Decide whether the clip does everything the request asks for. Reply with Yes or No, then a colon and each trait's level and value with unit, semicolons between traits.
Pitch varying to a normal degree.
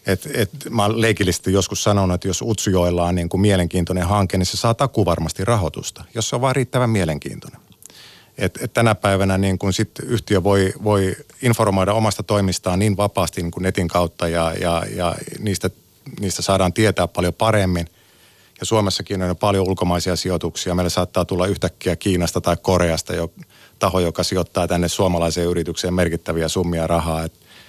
Yes: average, 3.0 semitones